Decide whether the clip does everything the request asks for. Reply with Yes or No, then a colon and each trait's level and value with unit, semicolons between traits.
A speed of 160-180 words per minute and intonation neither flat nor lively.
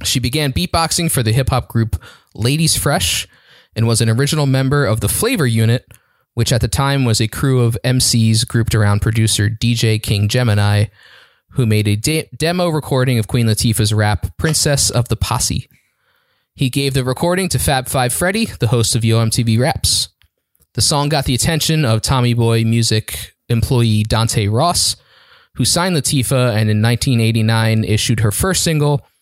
Yes: average, 175 wpm; average, 3.8 semitones